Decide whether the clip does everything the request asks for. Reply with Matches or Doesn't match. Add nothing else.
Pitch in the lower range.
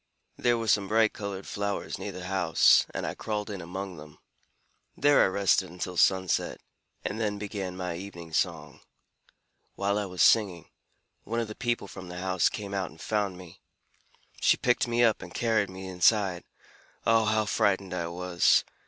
Matches